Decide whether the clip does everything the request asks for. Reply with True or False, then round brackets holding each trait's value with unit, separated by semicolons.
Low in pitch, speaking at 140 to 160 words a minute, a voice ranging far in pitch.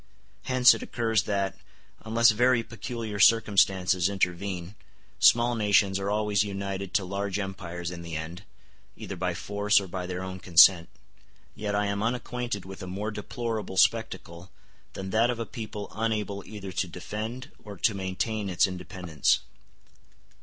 False (100 Hz; 150 wpm; 2.8 semitones)